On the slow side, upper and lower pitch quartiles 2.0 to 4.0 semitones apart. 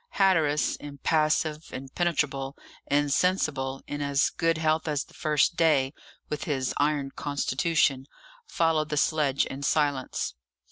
Yes: slow, 120 wpm; narrow, 2.4 semitones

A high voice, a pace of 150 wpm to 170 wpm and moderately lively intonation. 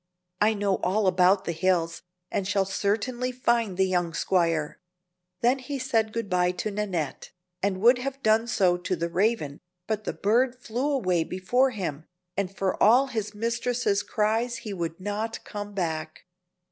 Yes: high, 205 Hz; average, 165 wpm; average, 4.2 semitones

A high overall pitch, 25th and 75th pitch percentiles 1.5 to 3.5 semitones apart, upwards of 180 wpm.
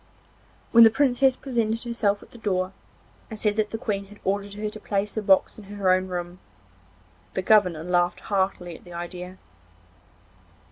No: high, 200 Hz; average, 2.9 semitones; average, 175 wpm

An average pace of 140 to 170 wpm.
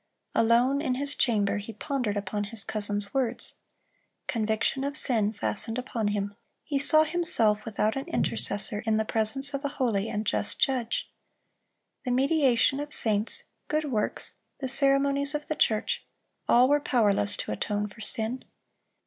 Yes: average, 155 wpm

